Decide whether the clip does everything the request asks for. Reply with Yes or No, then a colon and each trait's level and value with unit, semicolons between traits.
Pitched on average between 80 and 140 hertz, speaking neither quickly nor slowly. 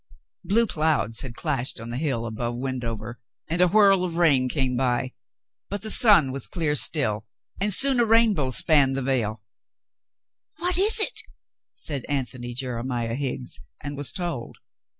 Yes: low, 135 Hz; average, 160 wpm